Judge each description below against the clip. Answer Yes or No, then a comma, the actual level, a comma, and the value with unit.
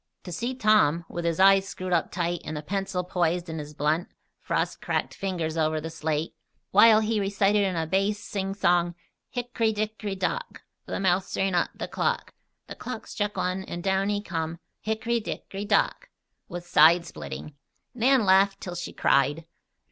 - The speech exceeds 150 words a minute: Yes, average, 175 wpm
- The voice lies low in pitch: No, high, 190 Hz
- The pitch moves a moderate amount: Yes, average, 3.5 semitones